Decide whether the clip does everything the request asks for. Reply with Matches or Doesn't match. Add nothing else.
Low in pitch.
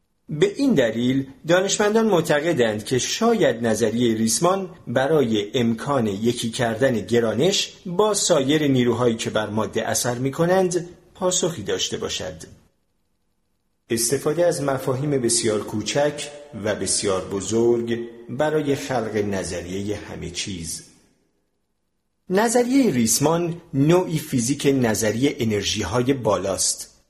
Matches